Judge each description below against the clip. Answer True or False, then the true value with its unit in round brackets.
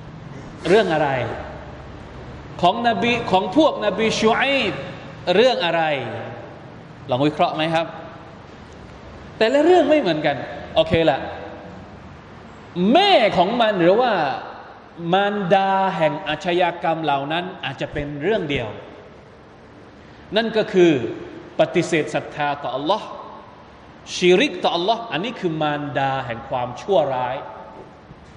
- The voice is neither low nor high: True (165 Hz)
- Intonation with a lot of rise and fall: True (5.7 semitones)